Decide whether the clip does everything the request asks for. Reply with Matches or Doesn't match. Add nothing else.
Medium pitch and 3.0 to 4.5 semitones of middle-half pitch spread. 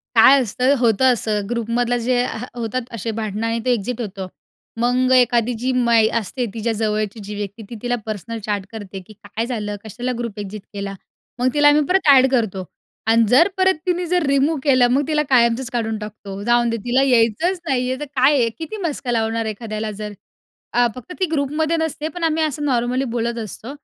Doesn't match